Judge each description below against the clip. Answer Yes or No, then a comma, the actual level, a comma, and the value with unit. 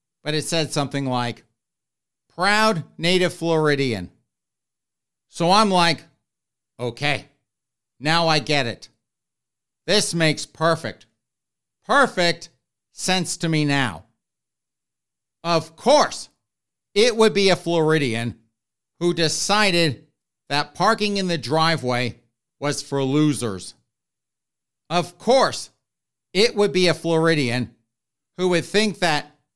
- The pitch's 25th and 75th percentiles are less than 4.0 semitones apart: No, average, 5.3 semitones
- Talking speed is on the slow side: Yes, slow, 105 wpm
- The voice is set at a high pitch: No, medium, 155 Hz